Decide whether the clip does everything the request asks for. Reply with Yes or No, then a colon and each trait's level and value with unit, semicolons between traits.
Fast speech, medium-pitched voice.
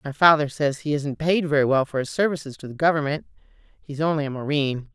Yes: fast, 220 wpm; medium, 145 Hz